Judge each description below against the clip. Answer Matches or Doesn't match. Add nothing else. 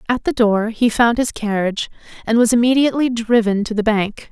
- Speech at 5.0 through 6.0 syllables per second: Matches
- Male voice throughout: Doesn't match